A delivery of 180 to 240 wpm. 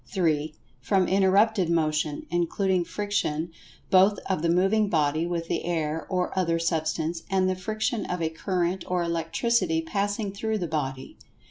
No: average, 150 wpm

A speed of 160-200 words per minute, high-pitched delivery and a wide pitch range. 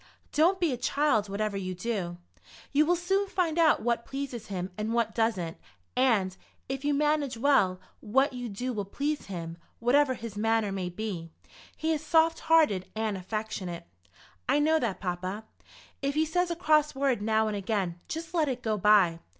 Yes: average, 180 wpm; high, 230 Hz; wide, 6.8 semitones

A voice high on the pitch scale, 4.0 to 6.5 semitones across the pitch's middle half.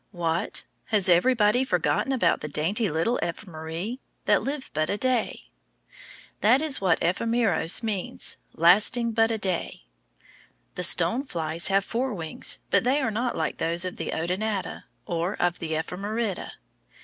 Yes: high, 195 Hz; wide, 5.4 semitones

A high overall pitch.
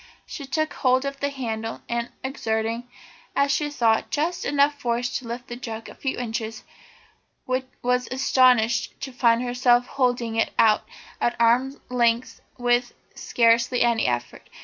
Yes: high, 245 Hz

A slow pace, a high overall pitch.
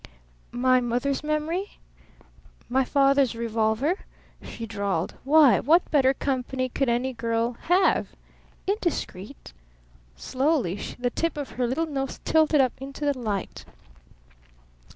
Yes: slow, 115 wpm; very high, 265 Hz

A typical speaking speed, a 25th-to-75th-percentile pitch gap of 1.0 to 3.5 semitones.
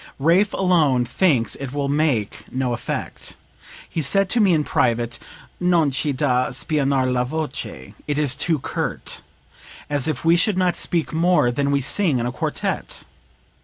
No: average, 165 wpm; average, 4.7 semitones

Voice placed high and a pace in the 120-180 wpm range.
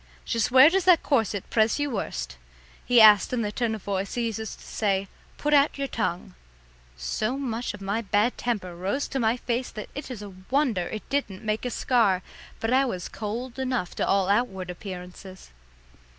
No: high, 220 Hz; average, 195 wpm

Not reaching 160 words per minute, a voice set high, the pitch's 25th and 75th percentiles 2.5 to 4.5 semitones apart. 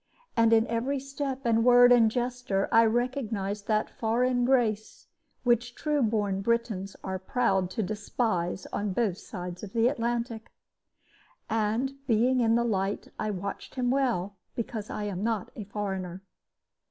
Yes: average, 150 wpm; high, 225 Hz; average, 3.4 semitones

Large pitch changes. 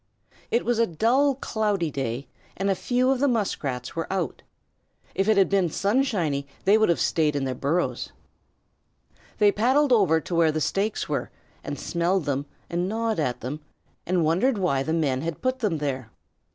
Yes: wide, 6.4 semitones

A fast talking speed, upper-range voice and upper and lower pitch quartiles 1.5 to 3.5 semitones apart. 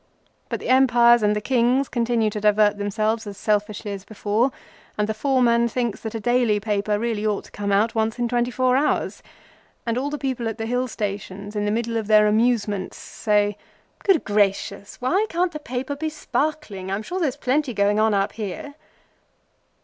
No: average, 190 wpm; high, 225 Hz; average, 3.2 semitones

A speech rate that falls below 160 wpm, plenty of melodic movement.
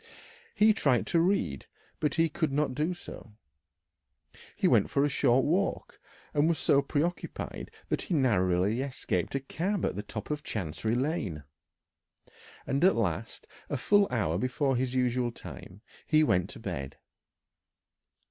Yes: average, 150 wpm; wide, 5.8 semitones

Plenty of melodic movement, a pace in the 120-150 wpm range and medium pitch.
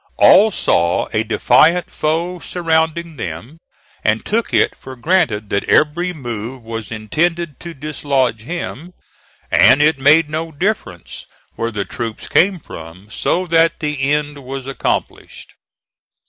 Yes: wide, 6.5 semitones; slow, 135 wpm; medium, 150 Hz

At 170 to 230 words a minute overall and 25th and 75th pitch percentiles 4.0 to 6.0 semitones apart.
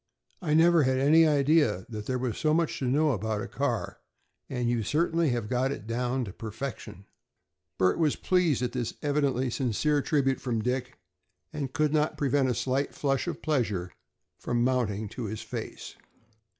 Yes: average, 175 wpm; average, 4.3 semitones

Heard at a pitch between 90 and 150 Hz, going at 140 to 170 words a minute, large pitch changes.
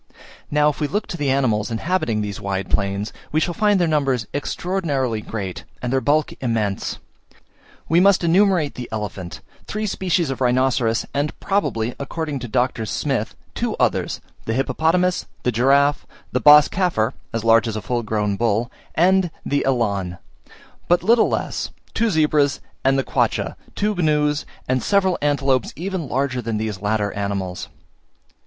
Yes: low, 135 Hz; average, 160 wpm; wide, 6.5 semitones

